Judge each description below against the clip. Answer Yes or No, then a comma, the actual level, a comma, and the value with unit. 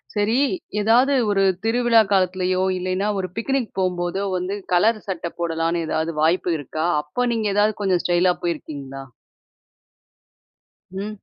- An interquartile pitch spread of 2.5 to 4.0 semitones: Yes, average, 3.7 semitones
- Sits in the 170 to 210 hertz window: Yes, medium, 185 Hz